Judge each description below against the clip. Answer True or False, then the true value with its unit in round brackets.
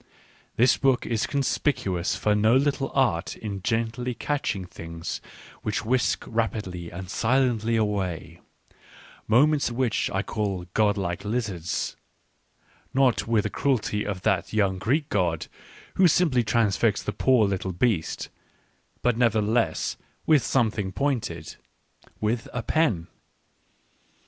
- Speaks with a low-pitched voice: True (110 Hz)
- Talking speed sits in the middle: False (125 wpm)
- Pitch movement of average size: True (4.4 semitones)